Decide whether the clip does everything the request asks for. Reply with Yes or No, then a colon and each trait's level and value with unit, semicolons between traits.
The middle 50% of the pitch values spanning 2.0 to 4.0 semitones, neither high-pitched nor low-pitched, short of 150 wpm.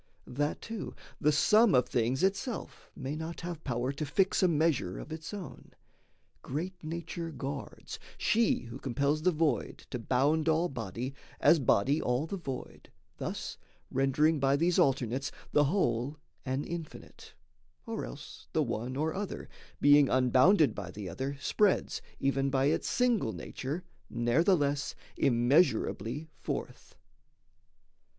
No: average, 4.4 semitones; medium, 145 Hz; slow, 135 wpm